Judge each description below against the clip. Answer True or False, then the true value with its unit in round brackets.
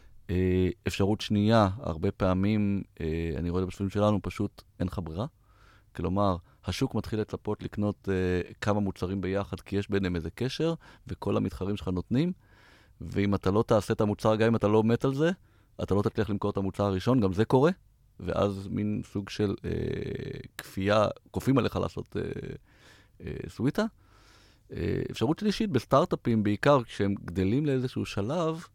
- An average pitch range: True (3.1 semitones)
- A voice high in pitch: False (105 Hz)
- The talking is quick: True (160 wpm)